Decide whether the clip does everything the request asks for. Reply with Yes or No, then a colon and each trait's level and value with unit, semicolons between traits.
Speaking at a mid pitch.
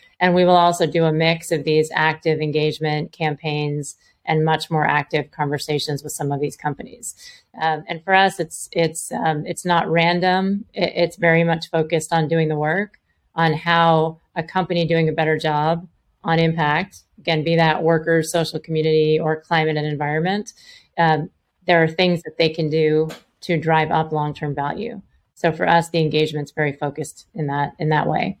Yes: medium, 160 Hz